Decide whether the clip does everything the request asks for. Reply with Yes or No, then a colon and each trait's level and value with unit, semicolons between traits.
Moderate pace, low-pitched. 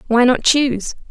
No: average, 165 wpm; very high, 250 Hz